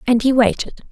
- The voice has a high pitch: Yes, high, 245 Hz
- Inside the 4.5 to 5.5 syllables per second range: Yes, 5.3 syllables/s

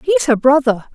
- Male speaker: No, female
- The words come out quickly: No, average, 190 wpm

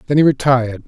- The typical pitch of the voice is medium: No, low, 130 Hz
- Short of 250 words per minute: Yes, fast, 205 wpm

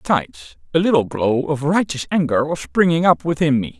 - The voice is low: No, medium, 145 Hz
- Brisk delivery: No, average, 190 wpm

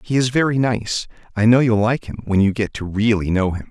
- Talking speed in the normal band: No, fast, 245 wpm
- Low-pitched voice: Yes, low, 110 Hz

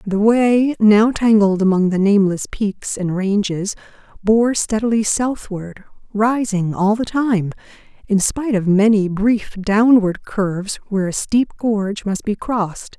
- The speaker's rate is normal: Yes, average, 145 wpm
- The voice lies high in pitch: Yes, high, 210 Hz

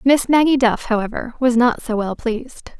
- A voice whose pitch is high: Yes, high, 240 Hz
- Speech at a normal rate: Yes, average, 195 wpm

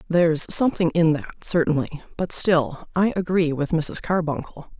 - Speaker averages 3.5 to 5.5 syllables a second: Yes, 4.8 syllables/s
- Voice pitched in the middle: Yes, medium, 165 Hz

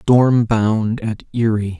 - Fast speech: No, slow, 135 wpm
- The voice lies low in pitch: Yes, low, 110 Hz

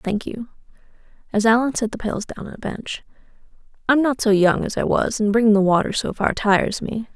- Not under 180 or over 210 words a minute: Yes, average, 200 wpm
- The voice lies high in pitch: Yes, high, 220 Hz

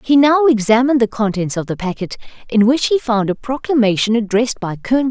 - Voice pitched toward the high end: Yes, high, 235 Hz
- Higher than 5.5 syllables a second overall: Yes, 5.7 syllables/s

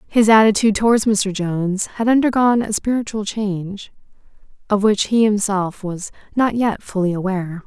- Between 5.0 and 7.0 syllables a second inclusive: Yes, 5.2 syllables/s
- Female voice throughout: Yes, female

